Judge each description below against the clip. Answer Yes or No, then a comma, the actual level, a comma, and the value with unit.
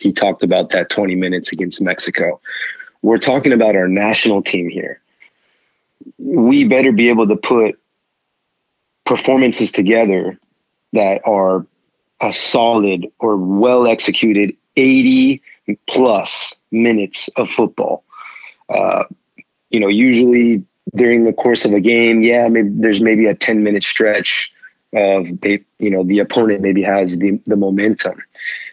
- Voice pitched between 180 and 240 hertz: No, low, 110 Hz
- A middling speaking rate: No, slow, 125 wpm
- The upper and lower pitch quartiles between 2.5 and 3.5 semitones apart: Yes, average, 3.1 semitones